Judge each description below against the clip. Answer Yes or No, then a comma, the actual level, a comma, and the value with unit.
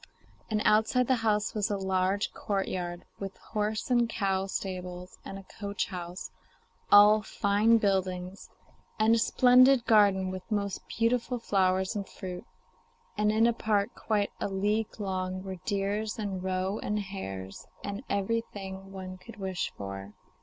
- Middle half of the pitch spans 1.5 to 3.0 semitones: Yes, narrow, 2.4 semitones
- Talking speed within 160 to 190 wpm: No, average, 145 wpm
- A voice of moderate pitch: No, high, 200 Hz